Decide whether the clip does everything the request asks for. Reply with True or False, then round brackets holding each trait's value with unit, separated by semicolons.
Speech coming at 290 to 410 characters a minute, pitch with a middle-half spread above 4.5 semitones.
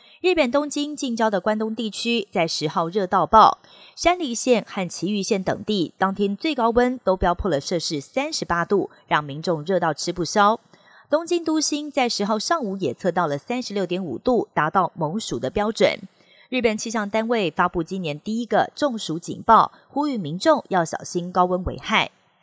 False (275 characters per minute; 5.4 semitones)